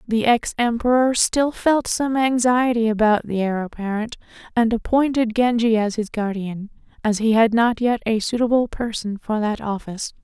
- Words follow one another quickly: No, average, 165 wpm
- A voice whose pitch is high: Yes, high, 230 Hz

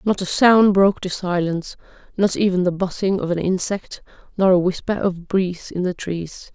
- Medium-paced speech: Yes, average, 195 wpm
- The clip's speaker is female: Yes, female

